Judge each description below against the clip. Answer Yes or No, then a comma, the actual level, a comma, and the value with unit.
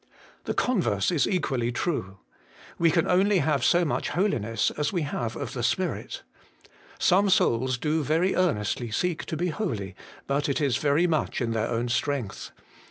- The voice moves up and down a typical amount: No, wide, 6.7 semitones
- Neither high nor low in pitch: Yes, medium, 145 Hz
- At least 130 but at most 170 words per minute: Yes, average, 165 wpm